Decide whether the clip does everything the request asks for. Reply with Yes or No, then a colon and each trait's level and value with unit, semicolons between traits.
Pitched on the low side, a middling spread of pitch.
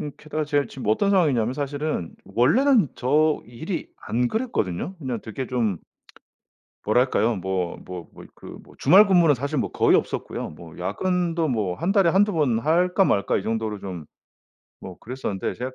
No: low, 130 Hz; wide, 7.6 semitones